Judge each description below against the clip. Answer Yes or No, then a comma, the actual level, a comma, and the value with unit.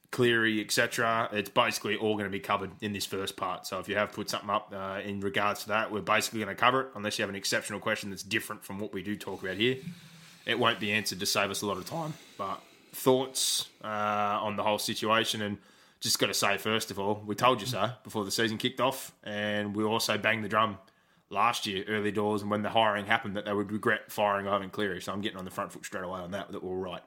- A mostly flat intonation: Yes, narrow, 1.9 semitones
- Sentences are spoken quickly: Yes, fast, 260 wpm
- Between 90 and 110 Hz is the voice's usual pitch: Yes, low, 105 Hz